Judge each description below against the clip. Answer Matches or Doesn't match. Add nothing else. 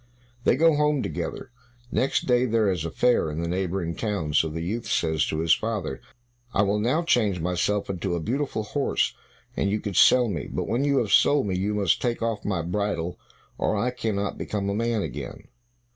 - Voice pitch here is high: Doesn't match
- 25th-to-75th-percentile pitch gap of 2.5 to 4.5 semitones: Doesn't match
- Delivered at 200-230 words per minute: Matches